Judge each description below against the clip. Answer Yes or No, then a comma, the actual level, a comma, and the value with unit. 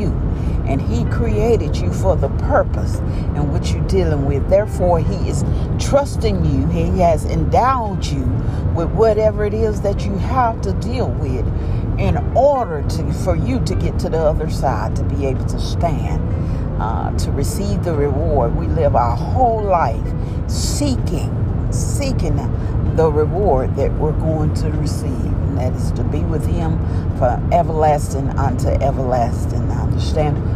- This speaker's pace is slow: No, average, 155 wpm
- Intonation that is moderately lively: Yes, average, 4.5 semitones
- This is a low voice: Yes, very low, 95 Hz